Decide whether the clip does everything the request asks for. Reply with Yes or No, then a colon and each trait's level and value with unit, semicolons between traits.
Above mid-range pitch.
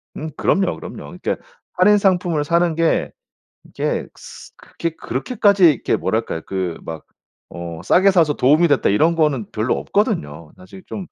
No: medium, 155 Hz